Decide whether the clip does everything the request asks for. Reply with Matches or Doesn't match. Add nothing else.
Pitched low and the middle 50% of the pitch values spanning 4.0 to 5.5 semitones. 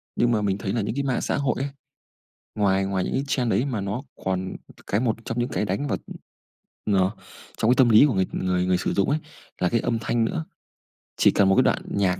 Matches